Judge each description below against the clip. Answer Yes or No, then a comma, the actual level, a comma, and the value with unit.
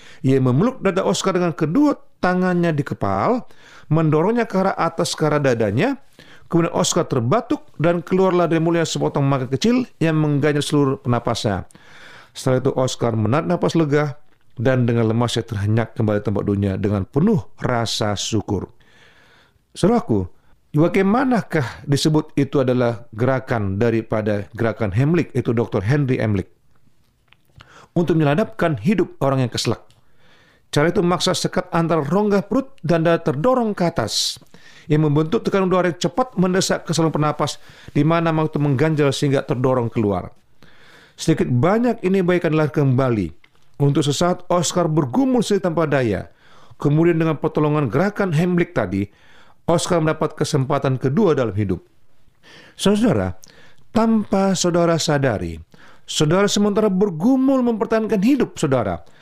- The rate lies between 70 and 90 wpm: No, average, 135 wpm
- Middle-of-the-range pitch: Yes, medium, 155 Hz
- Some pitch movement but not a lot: No, wide, 6.0 semitones